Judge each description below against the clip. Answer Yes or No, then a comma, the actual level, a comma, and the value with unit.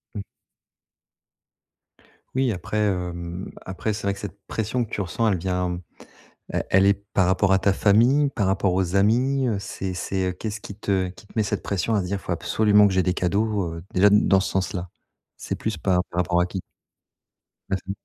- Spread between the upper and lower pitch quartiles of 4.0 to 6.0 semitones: No, narrow, 2.4 semitones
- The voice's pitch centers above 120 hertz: No, very low, 95 Hz